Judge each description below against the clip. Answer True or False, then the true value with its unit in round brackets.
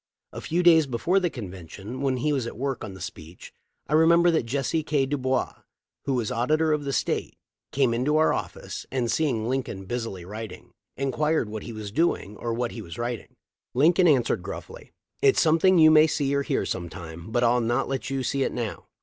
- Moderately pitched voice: False (130 Hz)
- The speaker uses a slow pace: False (200 wpm)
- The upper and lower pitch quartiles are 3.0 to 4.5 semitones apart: False (5.1 semitones)